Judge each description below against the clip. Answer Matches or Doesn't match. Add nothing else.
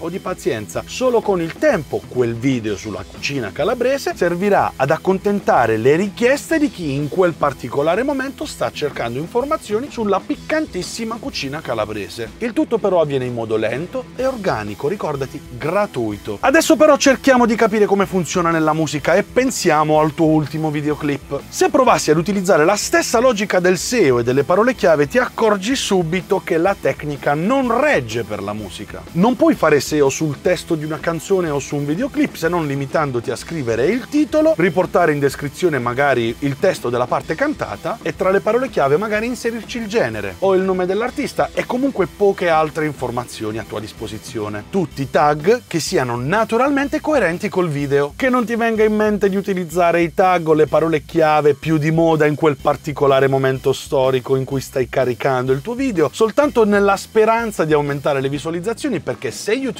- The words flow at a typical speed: Doesn't match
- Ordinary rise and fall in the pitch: Doesn't match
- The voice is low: Doesn't match